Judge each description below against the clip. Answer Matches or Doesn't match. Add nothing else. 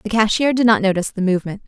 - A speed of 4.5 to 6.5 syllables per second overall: Doesn't match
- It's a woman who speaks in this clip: Matches